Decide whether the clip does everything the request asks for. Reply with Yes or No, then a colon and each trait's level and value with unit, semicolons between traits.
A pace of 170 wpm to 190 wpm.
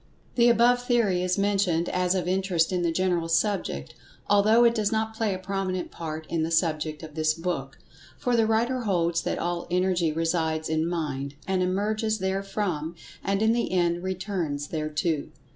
Yes: average, 175 wpm